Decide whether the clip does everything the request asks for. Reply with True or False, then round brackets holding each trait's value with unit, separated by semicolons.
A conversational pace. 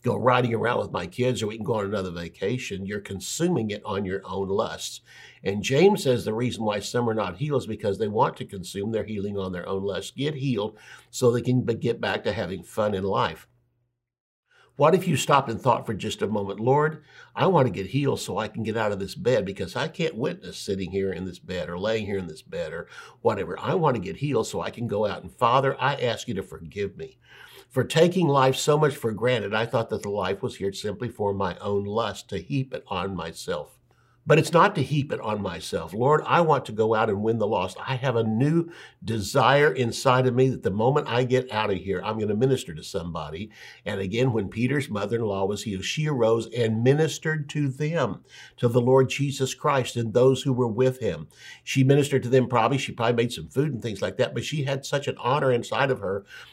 False (240 wpm)